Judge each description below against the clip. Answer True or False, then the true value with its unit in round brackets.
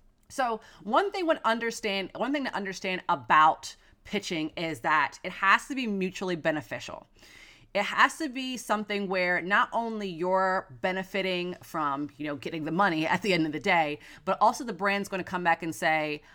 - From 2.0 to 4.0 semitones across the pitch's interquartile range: False (4.4 semitones)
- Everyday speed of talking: True (185 wpm)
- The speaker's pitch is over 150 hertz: True (190 Hz)